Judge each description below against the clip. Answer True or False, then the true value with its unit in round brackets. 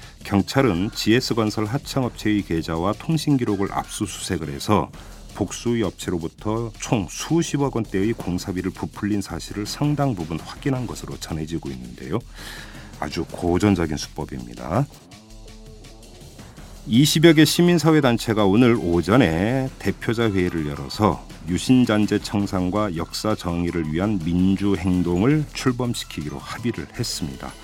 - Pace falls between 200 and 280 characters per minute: False (295 characters per minute)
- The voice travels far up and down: True (5.8 semitones)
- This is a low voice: True (105 Hz)